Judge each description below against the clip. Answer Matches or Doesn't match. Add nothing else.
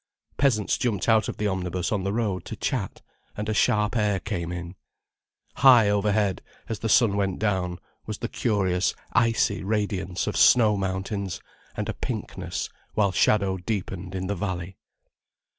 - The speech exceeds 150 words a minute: Matches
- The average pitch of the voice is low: Matches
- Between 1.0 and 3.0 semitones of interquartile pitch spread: Matches